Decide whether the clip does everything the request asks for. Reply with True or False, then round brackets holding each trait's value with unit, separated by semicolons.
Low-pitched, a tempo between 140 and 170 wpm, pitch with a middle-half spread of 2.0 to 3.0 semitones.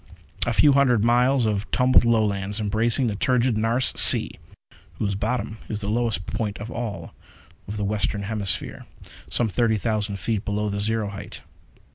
True (110 Hz; 155 wpm; 2.5 semitones)